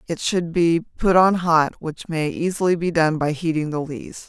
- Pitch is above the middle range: No, medium, 165 Hz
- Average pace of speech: No, fast, 210 wpm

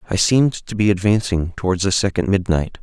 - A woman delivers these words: No, male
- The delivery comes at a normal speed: Yes, average, 190 wpm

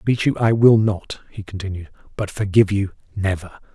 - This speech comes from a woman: No, male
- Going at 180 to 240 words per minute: No, average, 160 wpm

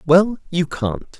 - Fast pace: No, average, 150 wpm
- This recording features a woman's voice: No, male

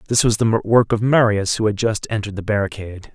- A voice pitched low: Yes, low, 105 Hz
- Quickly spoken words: Yes, fast, 230 wpm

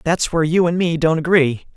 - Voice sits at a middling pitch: Yes, medium, 165 Hz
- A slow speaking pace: No, fast, 240 wpm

